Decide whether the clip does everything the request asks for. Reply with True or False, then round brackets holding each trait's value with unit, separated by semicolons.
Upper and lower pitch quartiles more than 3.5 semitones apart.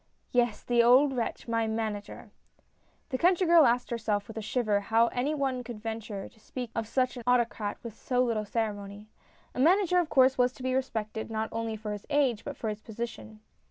False (2.8 semitones)